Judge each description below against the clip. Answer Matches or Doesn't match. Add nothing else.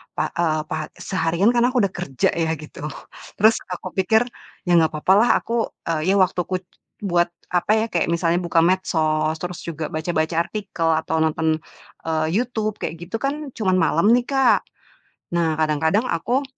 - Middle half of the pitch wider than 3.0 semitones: Matches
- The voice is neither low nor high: Matches